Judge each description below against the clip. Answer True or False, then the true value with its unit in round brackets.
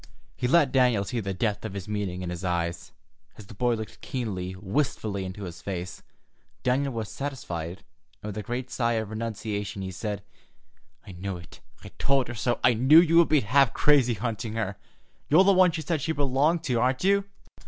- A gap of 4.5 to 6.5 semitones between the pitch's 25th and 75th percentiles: True (5.5 semitones)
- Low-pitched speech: True (115 Hz)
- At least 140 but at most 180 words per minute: False (200 wpm)